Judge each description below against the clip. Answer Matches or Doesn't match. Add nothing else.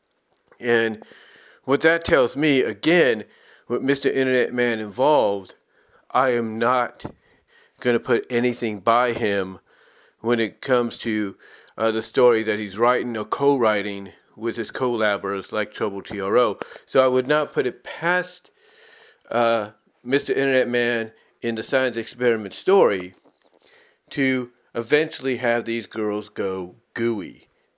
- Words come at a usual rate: Doesn't match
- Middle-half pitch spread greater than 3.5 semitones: Doesn't match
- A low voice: Matches